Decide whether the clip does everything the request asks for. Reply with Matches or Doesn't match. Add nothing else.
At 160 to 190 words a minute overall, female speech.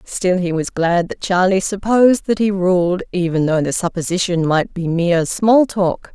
Matches